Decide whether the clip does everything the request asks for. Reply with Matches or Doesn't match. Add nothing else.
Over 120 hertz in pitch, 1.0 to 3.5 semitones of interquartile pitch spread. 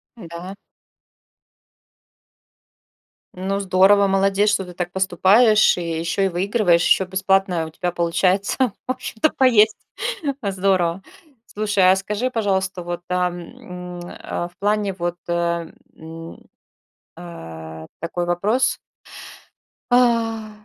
Matches